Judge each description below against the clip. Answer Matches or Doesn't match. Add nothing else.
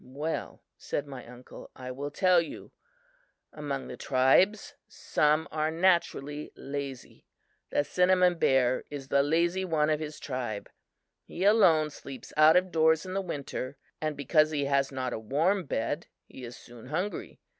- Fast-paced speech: Doesn't match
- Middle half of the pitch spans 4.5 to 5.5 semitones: Doesn't match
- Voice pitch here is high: Doesn't match